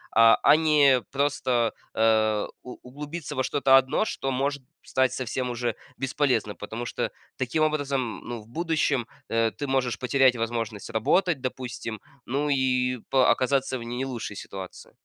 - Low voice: Yes, low, 130 Hz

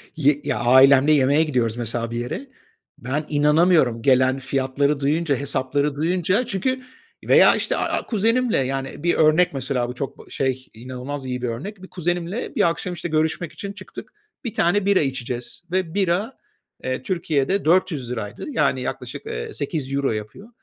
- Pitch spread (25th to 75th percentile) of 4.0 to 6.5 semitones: Yes, average, 5.2 semitones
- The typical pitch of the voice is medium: Yes, medium, 145 Hz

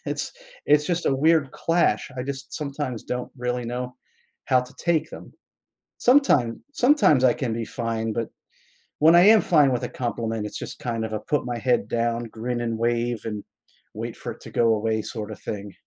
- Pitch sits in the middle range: No, low, 125 Hz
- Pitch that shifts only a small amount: No, average, 3.9 semitones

